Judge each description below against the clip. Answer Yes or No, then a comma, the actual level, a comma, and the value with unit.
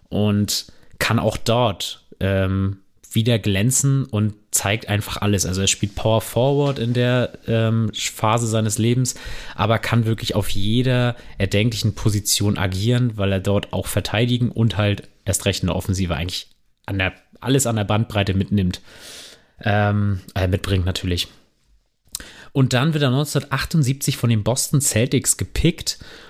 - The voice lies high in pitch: No, low, 105 Hz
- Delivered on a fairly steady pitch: No, average, 3.4 semitones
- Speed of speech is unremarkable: Yes, average, 145 wpm